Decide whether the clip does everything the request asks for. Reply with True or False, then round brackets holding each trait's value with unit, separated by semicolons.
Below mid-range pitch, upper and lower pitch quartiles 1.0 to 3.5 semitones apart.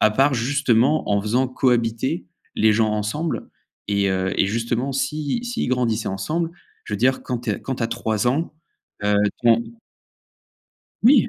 False (120 Hz; 4.2 semitones)